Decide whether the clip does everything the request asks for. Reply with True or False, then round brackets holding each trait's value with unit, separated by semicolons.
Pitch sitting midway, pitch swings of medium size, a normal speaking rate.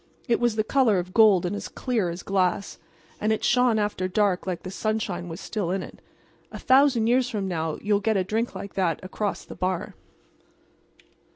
False (205 Hz; 3.2 semitones; 195 wpm)